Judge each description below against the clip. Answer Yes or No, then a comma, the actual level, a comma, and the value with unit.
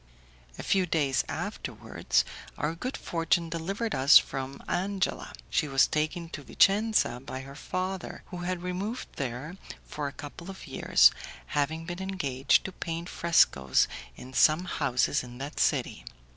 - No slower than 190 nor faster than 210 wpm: No, average, 145 wpm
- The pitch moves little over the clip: No, average, 5.0 semitones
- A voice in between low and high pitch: Yes, medium, 165 Hz